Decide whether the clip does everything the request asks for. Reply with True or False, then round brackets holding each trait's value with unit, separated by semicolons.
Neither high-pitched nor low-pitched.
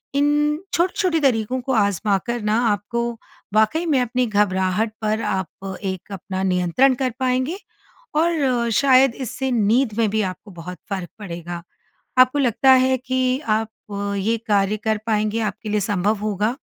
False (220 Hz)